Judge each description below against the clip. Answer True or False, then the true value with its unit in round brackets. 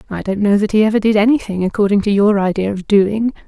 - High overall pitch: True (205 Hz)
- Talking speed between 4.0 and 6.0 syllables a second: False (6.3 syllables/s)